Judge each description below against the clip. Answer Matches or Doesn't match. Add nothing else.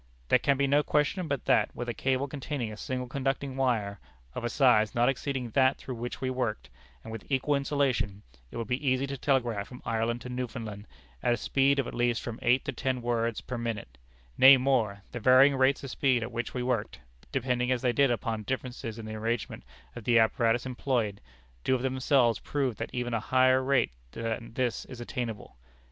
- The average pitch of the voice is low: Matches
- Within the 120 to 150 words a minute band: Doesn't match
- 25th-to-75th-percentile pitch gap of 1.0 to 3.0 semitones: Matches